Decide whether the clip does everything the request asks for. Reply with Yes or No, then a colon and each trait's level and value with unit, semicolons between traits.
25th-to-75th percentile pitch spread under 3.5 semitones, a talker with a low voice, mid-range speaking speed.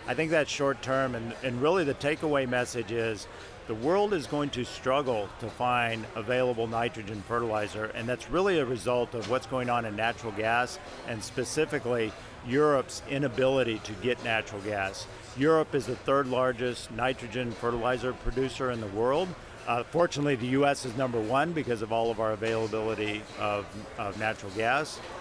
Yes: average, 2.9 semitones; low, 120 Hz; average, 170 wpm